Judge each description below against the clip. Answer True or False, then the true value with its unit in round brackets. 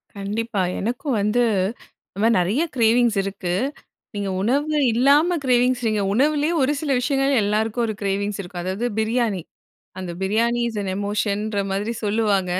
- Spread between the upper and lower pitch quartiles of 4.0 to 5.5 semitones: False (3.6 semitones)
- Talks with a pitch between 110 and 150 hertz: False (220 Hz)